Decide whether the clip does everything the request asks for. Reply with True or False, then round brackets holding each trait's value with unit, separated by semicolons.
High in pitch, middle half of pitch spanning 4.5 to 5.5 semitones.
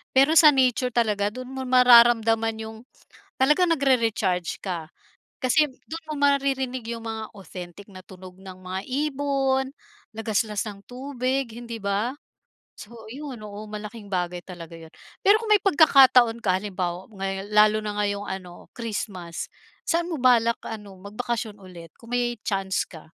True (225 Hz; 5.0 semitones)